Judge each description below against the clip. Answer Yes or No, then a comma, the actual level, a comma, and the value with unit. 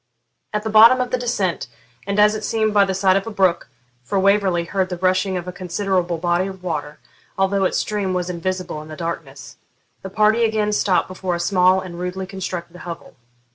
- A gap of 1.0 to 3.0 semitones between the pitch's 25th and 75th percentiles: Yes, narrow, 2.4 semitones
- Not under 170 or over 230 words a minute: Yes, fast, 205 wpm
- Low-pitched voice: No, medium, 185 Hz